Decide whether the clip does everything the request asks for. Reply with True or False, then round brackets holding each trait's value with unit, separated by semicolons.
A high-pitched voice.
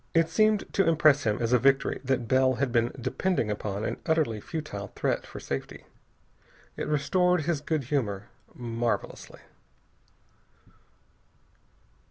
False (135 Hz)